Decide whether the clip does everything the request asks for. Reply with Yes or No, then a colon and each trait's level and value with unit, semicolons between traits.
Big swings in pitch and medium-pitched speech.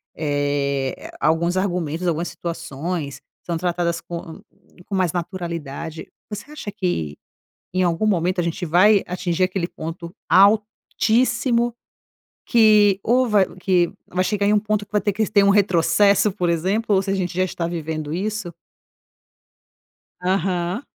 No: average, 3.4 semitones; medium, 180 Hz